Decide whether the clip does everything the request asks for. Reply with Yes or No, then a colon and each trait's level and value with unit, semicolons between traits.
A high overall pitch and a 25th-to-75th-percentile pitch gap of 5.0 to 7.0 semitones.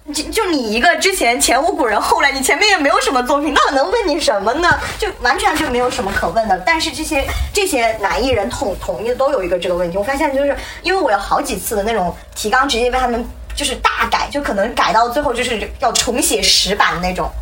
Yes: very high, 260 Hz; wide, 5.4 semitones